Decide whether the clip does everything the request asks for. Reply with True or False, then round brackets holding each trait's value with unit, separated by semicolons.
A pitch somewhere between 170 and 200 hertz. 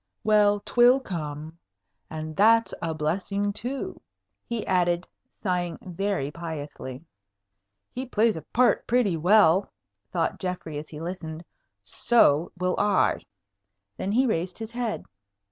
True (185 Hz)